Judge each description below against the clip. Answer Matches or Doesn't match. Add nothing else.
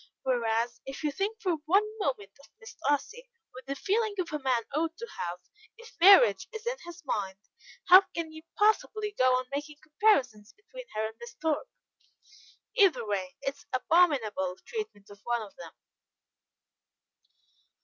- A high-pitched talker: Matches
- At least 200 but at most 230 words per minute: Doesn't match